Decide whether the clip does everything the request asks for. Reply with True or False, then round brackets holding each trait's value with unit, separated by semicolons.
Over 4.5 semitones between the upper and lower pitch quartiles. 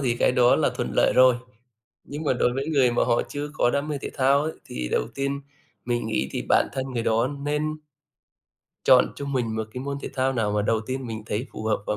False (3.6 semitones)